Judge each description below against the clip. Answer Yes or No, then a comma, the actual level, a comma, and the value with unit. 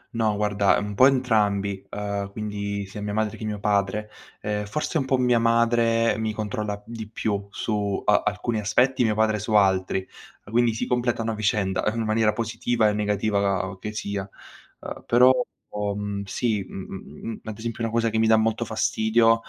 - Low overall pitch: Yes, low, 105 Hz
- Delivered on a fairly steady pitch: Yes, narrow, 2.0 semitones